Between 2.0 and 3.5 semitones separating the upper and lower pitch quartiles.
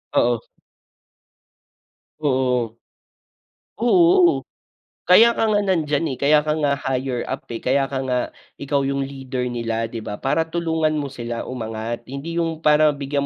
No: average, 4.2 semitones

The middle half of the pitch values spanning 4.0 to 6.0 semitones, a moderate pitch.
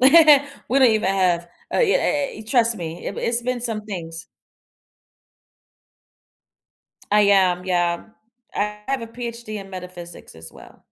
No: average, 5.1 semitones; high, 210 Hz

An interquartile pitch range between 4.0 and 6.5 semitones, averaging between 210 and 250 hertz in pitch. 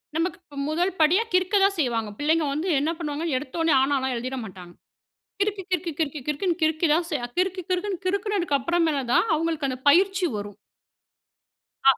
No: average, 4.5 semitones; very high, 325 Hz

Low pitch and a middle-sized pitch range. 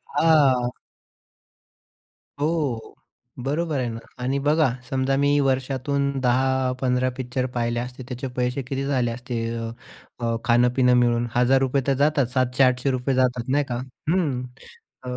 No: low, 130 Hz; narrow, 1.9 semitones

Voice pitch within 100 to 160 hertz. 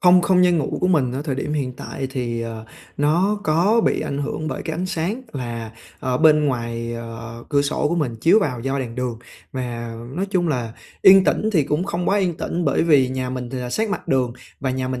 Yes: medium, 140 Hz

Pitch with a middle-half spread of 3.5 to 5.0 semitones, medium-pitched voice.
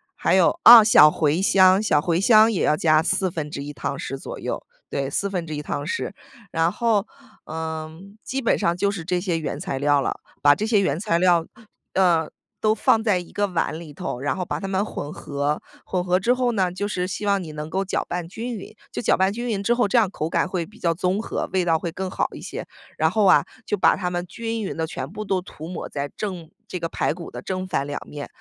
Yes: average, 4.0 semitones; medium, 180 Hz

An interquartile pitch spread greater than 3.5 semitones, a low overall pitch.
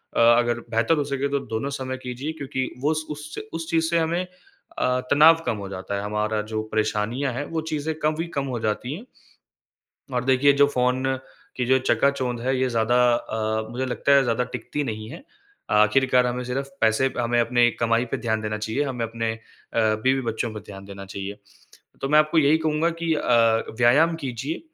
Yes: average, 4.2 semitones; low, 125 Hz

